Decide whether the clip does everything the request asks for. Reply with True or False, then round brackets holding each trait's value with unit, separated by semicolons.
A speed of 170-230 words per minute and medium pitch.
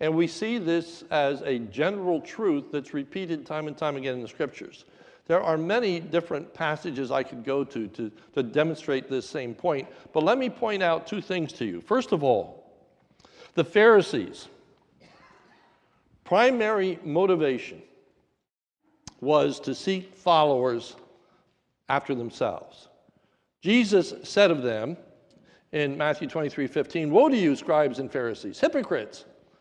False (140 wpm; 160 Hz)